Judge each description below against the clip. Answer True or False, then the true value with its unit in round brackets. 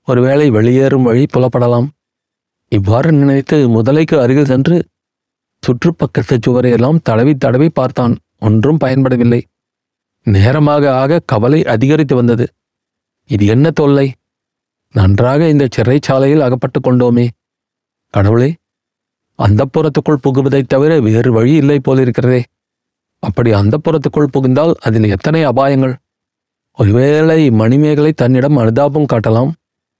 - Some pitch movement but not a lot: True (3.7 semitones)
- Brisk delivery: False (95 wpm)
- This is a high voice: False (130 Hz)